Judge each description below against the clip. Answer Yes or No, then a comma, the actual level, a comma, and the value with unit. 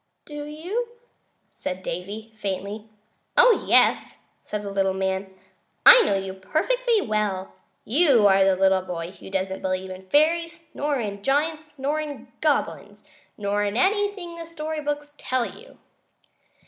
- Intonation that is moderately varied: No, wide, 8.4 semitones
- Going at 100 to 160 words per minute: Yes, average, 145 wpm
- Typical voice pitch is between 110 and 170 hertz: No, high, 225 Hz